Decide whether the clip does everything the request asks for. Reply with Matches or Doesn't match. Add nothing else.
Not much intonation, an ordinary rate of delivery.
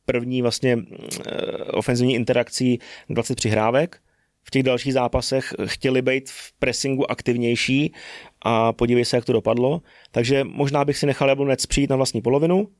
Matches